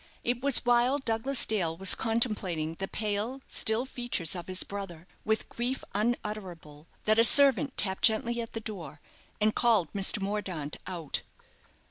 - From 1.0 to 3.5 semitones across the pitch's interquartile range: No, average, 4.4 semitones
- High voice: Yes, high, 215 Hz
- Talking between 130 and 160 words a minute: Yes, average, 150 wpm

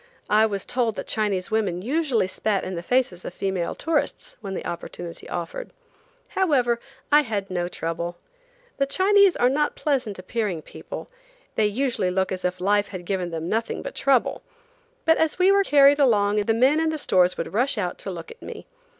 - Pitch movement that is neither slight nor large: No, wide, 7.1 semitones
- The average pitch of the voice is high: Yes, high, 215 Hz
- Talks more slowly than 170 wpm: No, average, 190 wpm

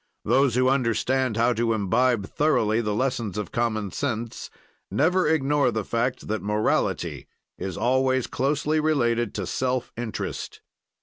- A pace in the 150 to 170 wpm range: No, slow, 135 wpm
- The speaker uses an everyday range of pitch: Yes, average, 3.3 semitones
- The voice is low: Yes, low, 120 Hz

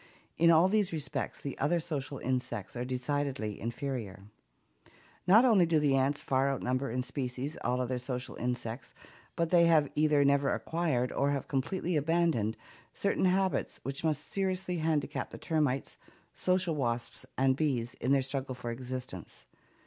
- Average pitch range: Yes, average, 4.3 semitones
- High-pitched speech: No, medium, 140 Hz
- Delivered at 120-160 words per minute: Yes, average, 155 wpm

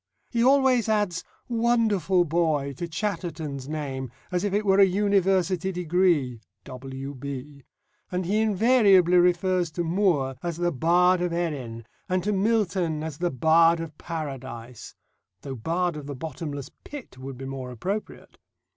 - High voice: No, medium, 170 Hz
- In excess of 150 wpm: No, average, 145 wpm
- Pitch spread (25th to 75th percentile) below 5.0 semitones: No, average, 5.3 semitones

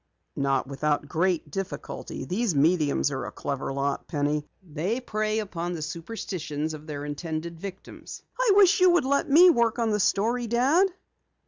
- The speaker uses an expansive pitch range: Yes, wide, 7.4 semitones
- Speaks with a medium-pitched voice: Yes, medium, 175 Hz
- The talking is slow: No, average, 160 wpm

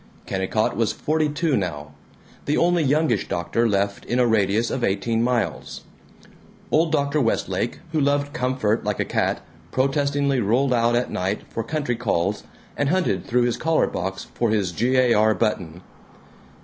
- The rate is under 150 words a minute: No, average, 160 wpm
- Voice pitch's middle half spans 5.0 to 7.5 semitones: Yes, wide, 5.5 semitones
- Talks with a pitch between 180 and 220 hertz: No, low, 120 Hz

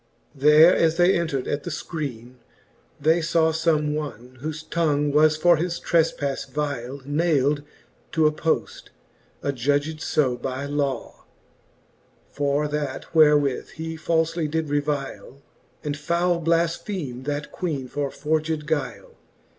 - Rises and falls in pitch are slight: Yes, narrow, 2.2 semitones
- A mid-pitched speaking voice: Yes, medium, 150 Hz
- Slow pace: Yes, slow, 125 wpm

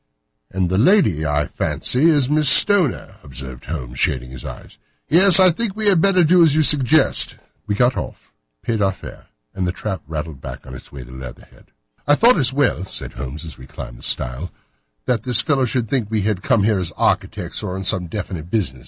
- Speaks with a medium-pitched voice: No, low, 105 Hz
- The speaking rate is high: Yes, fast, 215 wpm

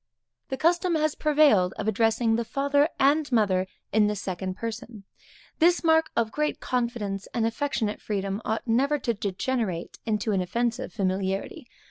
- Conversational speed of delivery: Yes, average, 150 wpm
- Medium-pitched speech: No, high, 230 Hz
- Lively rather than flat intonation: Yes, wide, 5.9 semitones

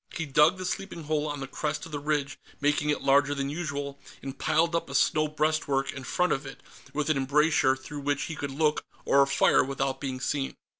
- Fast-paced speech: Yes, fast, 215 wpm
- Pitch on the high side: No, medium, 145 Hz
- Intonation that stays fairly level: Yes, narrow, 2.0 semitones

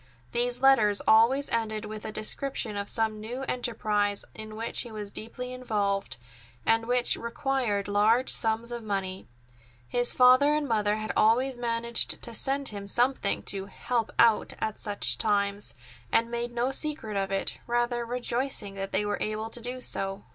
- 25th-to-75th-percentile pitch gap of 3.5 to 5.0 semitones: No, average, 2.8 semitones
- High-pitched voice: Yes, high, 225 Hz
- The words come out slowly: No, average, 165 wpm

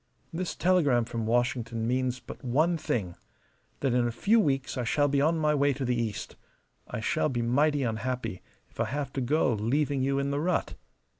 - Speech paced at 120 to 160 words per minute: No, average, 200 wpm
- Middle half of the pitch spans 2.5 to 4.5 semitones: Yes, average, 3.6 semitones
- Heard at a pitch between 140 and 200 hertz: No, low, 130 Hz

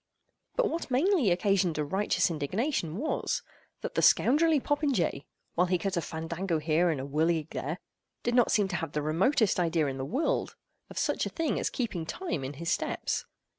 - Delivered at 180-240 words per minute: Yes, average, 190 wpm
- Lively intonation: Yes, wide, 7.9 semitones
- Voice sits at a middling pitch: Yes, medium, 180 Hz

